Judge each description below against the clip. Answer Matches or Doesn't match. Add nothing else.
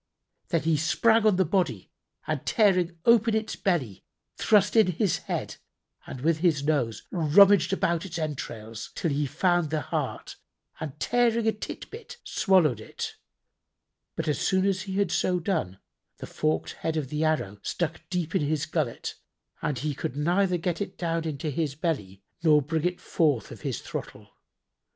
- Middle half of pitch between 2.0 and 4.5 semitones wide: Matches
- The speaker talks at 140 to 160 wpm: Doesn't match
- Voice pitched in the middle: Matches